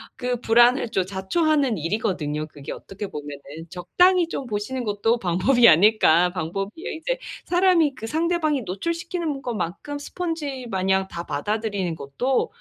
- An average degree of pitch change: No, wide, 7.9 semitones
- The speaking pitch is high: Yes, high, 225 Hz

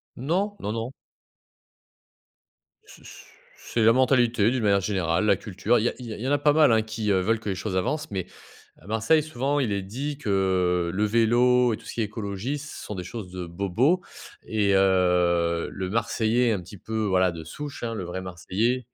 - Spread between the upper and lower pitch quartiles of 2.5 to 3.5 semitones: No, average, 4.7 semitones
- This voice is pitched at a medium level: No, low, 110 Hz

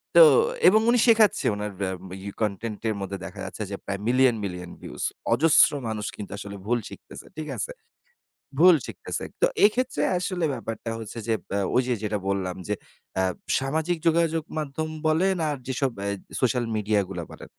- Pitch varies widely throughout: Yes, wide, 7.9 semitones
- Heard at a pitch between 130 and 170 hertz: No, low, 120 Hz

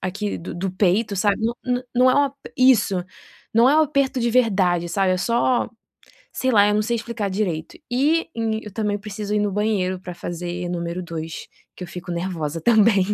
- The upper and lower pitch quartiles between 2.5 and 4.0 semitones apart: No, average, 4.6 semitones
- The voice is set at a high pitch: Yes, high, 205 Hz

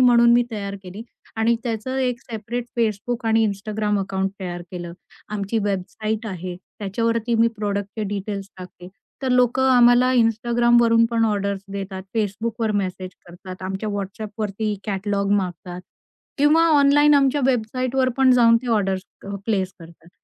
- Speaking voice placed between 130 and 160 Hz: No, high, 215 Hz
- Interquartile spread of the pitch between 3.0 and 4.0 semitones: Yes, average, 3.4 semitones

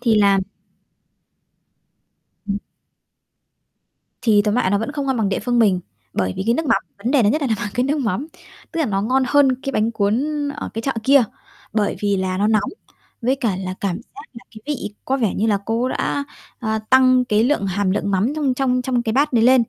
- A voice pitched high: Yes, high, 230 Hz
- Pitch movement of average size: Yes, average, 4.3 semitones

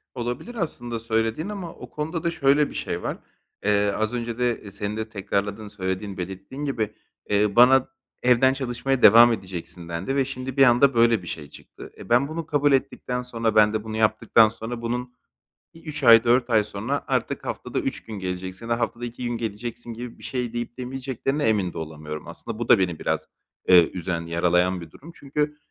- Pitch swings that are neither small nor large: Yes, average, 4.2 semitones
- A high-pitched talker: No, low, 115 Hz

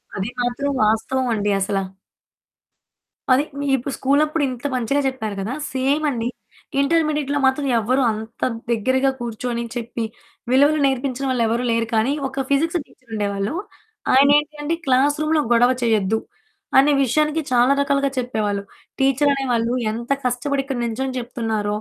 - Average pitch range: Yes, average, 3.5 semitones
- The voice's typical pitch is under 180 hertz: No, very high, 255 Hz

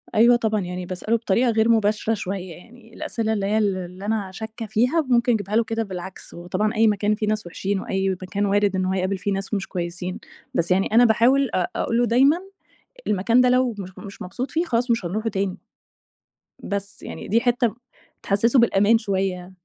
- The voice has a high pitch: Yes, high, 210 Hz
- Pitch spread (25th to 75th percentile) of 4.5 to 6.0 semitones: No, average, 3.3 semitones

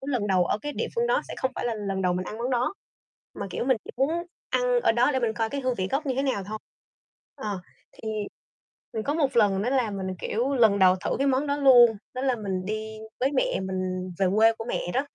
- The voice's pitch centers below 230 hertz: No, high, 235 Hz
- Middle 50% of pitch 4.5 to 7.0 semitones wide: Yes, average, 5.1 semitones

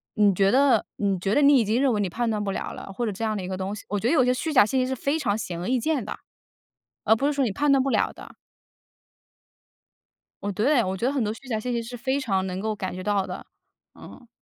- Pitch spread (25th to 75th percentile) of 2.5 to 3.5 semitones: No, average, 4.8 semitones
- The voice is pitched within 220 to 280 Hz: Yes, high, 225 Hz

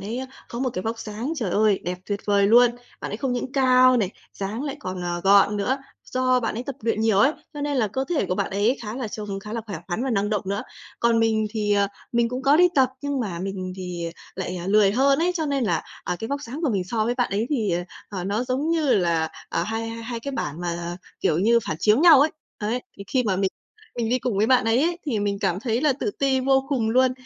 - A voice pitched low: No, high, 225 Hz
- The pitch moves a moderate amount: Yes, average, 4.5 semitones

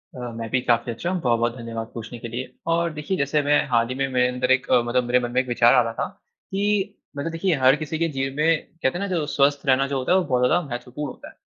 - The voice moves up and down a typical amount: Yes, average, 3.9 semitones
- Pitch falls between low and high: No, low, 130 Hz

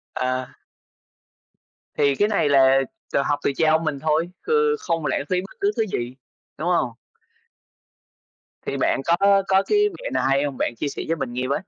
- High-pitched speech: No, medium, 155 Hz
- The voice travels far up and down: Yes, wide, 5.9 semitones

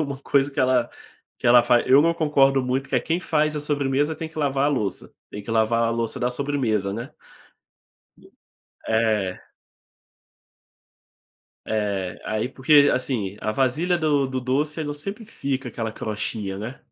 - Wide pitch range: No, average, 4.5 semitones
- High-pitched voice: No, low, 130 Hz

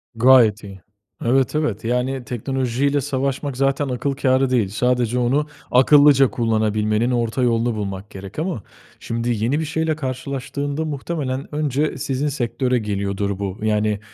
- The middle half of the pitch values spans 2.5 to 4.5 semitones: Yes, average, 4.0 semitones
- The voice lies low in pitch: Yes, low, 125 Hz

